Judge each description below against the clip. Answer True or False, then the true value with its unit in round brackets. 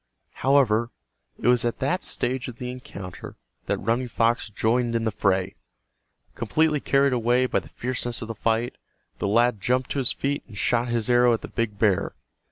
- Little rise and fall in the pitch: True (2.0 semitones)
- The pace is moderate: True (185 wpm)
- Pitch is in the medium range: False (120 Hz)